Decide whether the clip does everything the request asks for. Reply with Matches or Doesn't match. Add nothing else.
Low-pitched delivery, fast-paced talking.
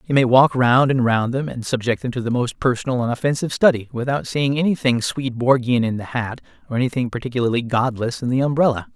Matches